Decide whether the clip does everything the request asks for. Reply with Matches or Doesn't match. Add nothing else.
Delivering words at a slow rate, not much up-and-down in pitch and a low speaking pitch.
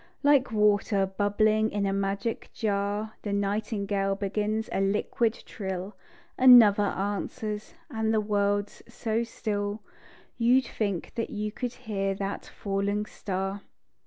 Doesn't match